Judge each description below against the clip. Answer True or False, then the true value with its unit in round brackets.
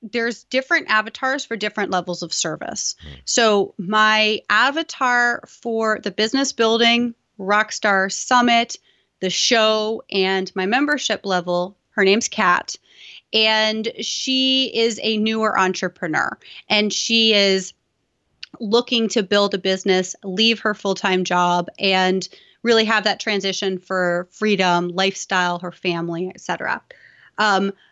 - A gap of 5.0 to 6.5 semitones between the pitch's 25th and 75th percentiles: False (3.3 semitones)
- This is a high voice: True (210 Hz)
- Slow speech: True (120 wpm)